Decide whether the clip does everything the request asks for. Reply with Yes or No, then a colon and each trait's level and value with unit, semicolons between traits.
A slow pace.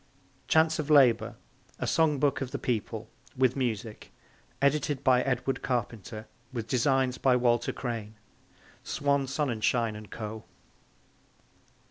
Yes: slow, 120 wpm